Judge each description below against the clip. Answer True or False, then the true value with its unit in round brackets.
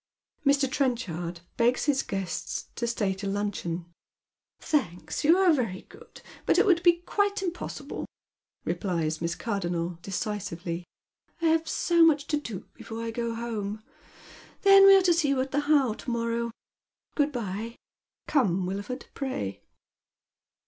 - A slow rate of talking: False (155 wpm)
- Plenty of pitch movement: True (7.6 semitones)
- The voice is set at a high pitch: True (235 Hz)